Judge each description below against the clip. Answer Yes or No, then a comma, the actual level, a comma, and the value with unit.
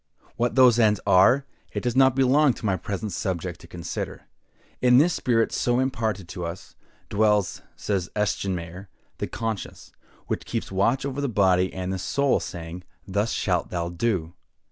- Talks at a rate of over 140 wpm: Yes, average, 165 wpm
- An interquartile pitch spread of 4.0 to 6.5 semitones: Yes, average, 5.1 semitones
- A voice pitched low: Yes, low, 105 Hz